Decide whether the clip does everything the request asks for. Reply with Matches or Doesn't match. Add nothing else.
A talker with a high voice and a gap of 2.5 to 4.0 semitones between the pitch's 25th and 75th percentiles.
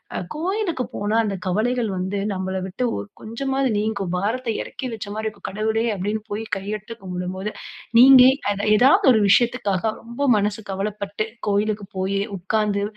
Matches